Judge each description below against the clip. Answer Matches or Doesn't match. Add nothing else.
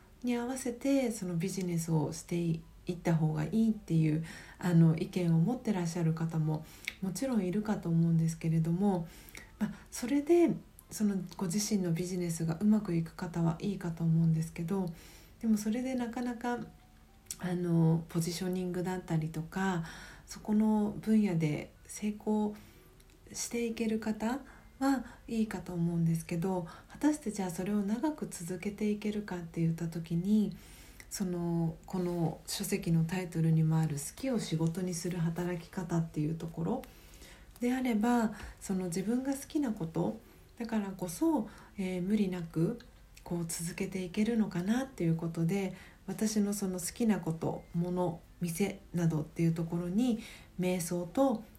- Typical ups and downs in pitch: Matches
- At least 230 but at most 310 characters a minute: Matches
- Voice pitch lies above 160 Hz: Matches